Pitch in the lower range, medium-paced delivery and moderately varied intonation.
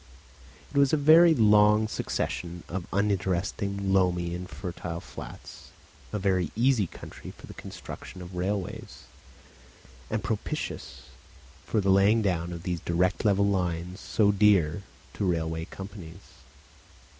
No: very low, 95 Hz; slow, 130 wpm; average, 3.0 semitones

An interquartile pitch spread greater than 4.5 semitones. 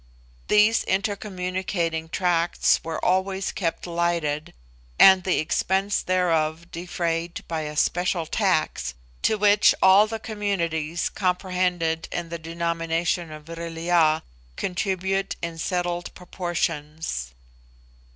No: narrow, 2.4 semitones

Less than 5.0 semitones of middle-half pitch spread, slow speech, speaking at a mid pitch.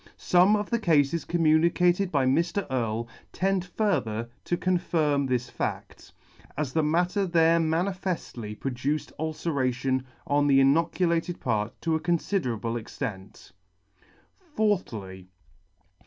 No: wide, 5.5 semitones; slow, 110 wpm; medium, 155 Hz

